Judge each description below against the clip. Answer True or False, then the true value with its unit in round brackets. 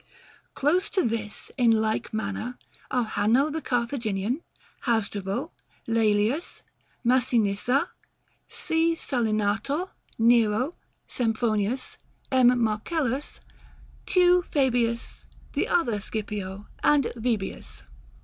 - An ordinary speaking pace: False (85 wpm)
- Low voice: False (235 Hz)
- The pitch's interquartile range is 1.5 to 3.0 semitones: False (4.1 semitones)